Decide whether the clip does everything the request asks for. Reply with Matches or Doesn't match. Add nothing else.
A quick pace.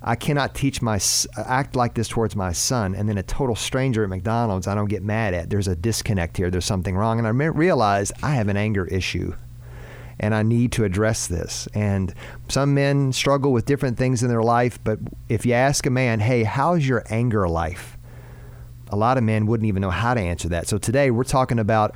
Matches